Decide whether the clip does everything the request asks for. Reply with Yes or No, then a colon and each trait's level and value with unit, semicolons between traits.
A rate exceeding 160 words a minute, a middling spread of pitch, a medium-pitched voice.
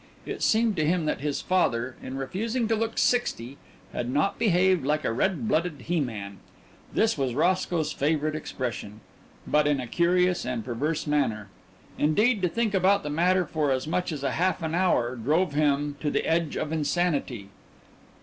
Yes: average, 180 wpm; average, 5.0 semitones; medium, 155 Hz